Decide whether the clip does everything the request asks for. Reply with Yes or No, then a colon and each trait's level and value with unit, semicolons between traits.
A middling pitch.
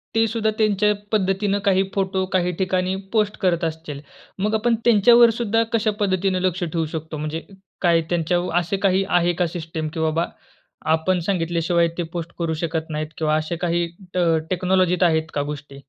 Yes: medium, 180 Hz